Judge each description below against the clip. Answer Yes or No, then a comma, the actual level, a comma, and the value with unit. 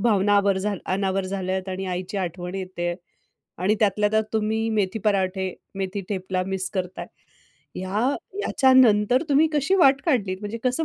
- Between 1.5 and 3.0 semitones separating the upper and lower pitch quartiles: Yes, average, 2.7 semitones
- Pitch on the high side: Yes, high, 195 Hz